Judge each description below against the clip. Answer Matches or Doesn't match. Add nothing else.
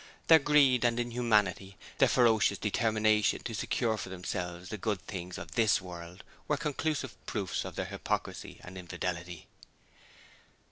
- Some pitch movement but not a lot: Matches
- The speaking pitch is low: Matches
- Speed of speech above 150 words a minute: Doesn't match